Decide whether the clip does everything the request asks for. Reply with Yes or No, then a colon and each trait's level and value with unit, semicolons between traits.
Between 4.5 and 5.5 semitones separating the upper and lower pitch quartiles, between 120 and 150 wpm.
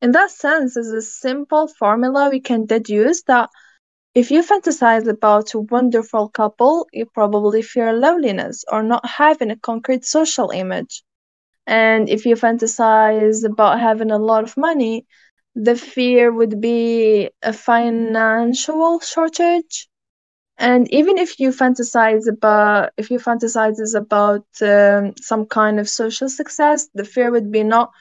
No: average, 3.1 semitones; average, 145 wpm